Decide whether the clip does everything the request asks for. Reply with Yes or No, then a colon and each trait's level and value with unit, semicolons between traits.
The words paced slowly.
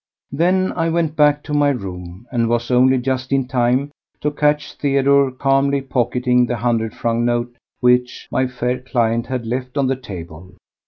No: average, 170 wpm